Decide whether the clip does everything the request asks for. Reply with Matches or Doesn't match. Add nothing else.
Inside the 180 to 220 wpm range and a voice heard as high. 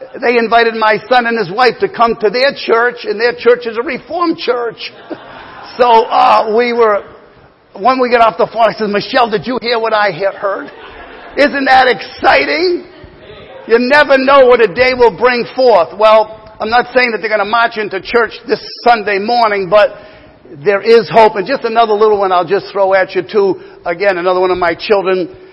Matches